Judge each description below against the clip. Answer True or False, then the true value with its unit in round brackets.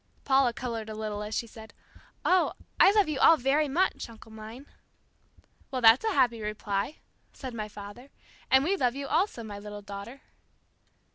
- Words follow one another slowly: False (170 wpm)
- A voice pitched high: True (235 Hz)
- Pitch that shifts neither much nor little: True (4.5 semitones)